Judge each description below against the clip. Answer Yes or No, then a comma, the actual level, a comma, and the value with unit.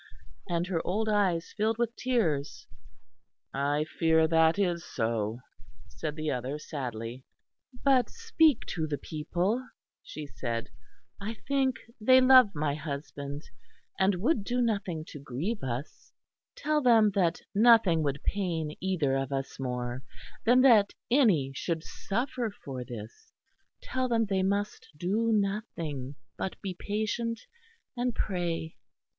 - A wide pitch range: Yes, wide, 7.5 semitones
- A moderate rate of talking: No, slow, 130 wpm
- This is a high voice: No, medium, 180 Hz